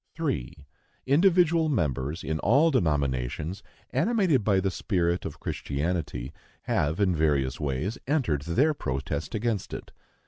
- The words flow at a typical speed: No, slow, 125 wpm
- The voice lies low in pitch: Yes, very low, 85 Hz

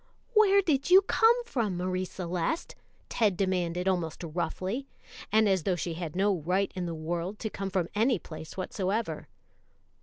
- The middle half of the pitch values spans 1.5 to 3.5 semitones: No, average, 4.0 semitones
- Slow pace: No, average, 160 wpm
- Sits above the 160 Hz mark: Yes, high, 190 Hz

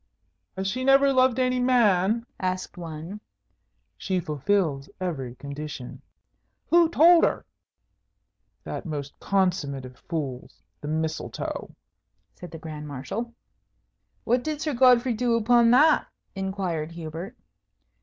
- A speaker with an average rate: No, slow, 115 wpm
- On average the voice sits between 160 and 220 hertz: Yes, high, 190 Hz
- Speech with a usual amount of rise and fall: No, wide, 8.1 semitones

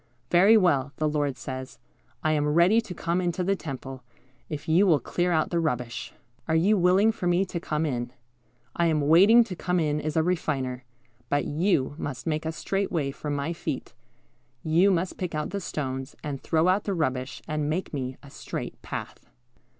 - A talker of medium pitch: Yes, medium, 160 Hz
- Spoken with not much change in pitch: No, average, 4.0 semitones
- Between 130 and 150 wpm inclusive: No, average, 195 wpm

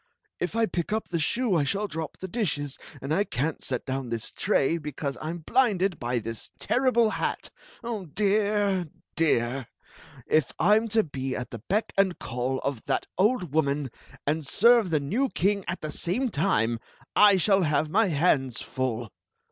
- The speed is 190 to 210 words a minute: No, average, 180 wpm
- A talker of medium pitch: Yes, medium, 165 Hz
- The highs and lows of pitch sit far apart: Yes, wide, 7.2 semitones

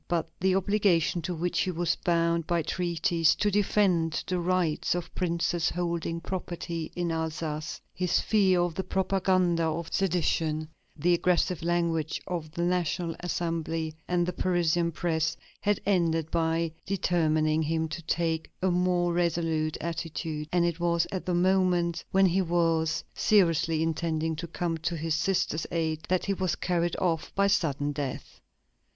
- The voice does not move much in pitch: Yes, narrow, 1.7 semitones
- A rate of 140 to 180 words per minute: Yes, average, 155 wpm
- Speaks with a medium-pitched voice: Yes, medium, 170 Hz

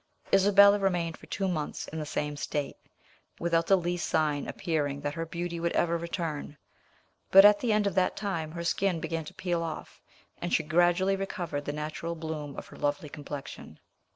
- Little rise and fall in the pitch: No, average, 3.4 semitones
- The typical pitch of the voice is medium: Yes, medium, 170 Hz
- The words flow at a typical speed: Yes, average, 185 wpm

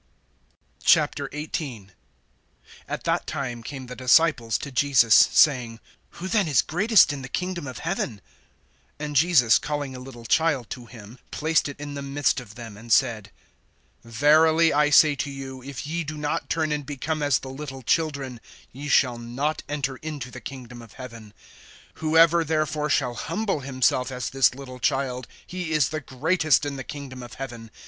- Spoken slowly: No, average, 170 wpm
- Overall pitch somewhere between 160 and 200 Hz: No, medium, 140 Hz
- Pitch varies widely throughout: No, average, 3.4 semitones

